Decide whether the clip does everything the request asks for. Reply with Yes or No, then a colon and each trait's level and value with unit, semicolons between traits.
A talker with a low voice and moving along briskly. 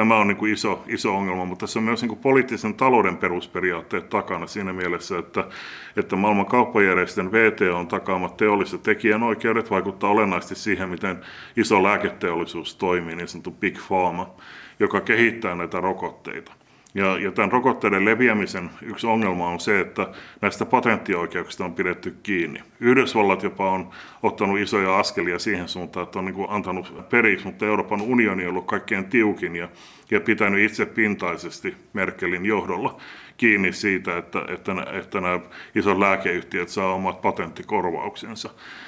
No: very low, 95 Hz; average, 135 wpm